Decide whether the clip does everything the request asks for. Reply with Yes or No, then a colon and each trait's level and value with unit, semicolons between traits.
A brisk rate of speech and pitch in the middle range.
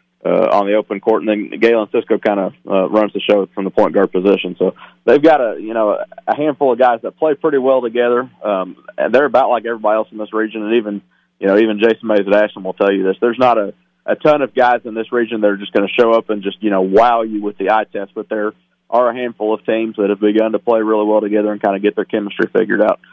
No: fast, 275 wpm; low, 110 Hz